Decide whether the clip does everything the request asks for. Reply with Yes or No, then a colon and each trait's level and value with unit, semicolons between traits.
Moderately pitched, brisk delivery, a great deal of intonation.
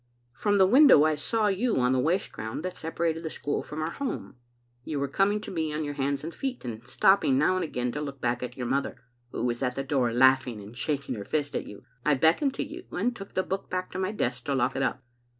Yes: medium, 145 Hz; fast, 260 wpm; wide, 6.6 semitones